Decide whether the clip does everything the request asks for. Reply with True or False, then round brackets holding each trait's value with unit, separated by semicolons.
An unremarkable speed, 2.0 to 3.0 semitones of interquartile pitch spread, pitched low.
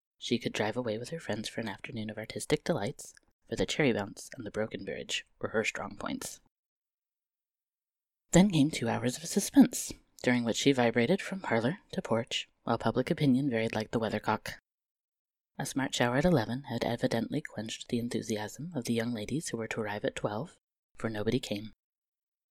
False (185 wpm; 4.1 semitones; 120 Hz)